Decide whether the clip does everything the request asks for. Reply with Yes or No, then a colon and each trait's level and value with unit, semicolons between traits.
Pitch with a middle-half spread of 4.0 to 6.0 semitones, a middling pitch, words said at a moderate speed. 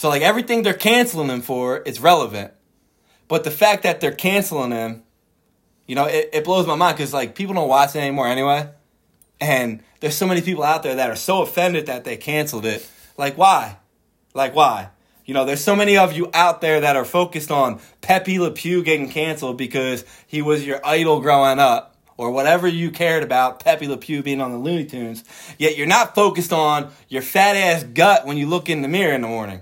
No: average, 4.9 semitones; medium, 150 Hz; fast, 210 wpm